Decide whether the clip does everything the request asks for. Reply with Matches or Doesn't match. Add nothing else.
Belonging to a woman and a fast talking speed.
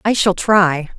Doesn't match